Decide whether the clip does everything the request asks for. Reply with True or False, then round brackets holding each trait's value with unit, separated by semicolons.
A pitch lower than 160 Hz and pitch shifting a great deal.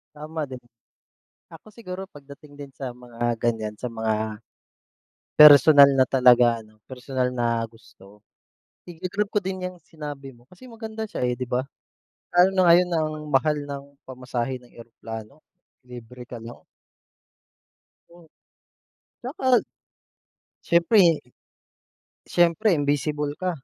True (140 Hz; 5.9 semitones)